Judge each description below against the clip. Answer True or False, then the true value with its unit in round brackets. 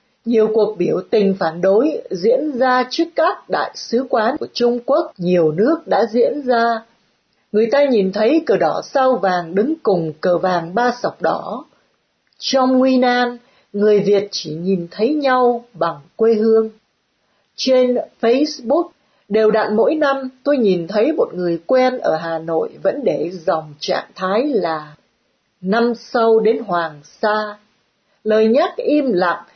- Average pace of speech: False (160 wpm)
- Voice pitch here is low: False (225 Hz)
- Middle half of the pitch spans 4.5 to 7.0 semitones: True (5.3 semitones)